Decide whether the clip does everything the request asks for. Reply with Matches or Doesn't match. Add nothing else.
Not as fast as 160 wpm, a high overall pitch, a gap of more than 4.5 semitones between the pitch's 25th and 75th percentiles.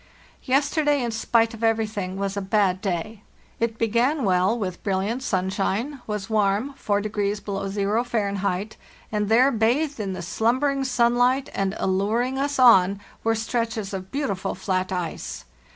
Doesn't match